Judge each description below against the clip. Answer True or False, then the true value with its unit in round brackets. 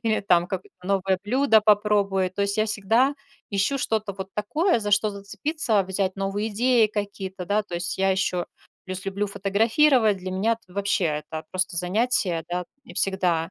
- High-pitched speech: True (200 Hz)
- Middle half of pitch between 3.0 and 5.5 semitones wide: False (2.5 semitones)